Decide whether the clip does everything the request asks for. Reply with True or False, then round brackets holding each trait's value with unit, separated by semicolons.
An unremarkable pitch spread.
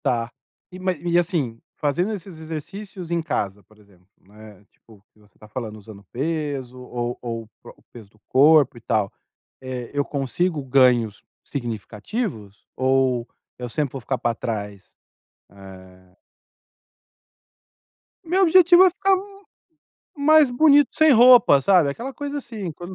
False (9.0 semitones)